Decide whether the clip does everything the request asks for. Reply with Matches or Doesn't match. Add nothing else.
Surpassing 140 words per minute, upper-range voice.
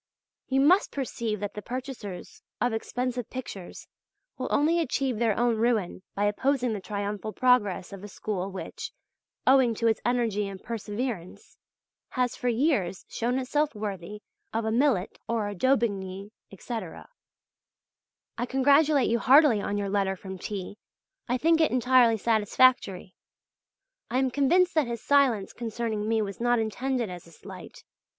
Matches